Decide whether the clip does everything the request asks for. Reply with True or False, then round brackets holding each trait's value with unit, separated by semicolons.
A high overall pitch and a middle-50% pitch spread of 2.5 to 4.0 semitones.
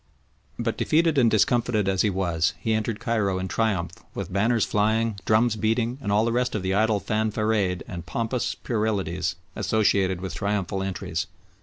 False (105 Hz; 2.9 semitones)